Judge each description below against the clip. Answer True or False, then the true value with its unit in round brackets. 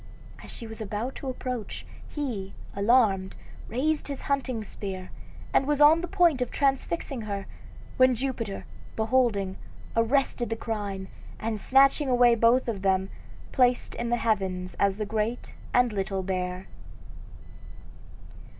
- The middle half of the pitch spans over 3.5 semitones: True (4.6 semitones)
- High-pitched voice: True (230 Hz)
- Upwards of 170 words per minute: False (140 wpm)